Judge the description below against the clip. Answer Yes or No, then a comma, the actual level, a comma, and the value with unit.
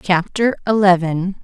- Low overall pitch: No, high, 190 Hz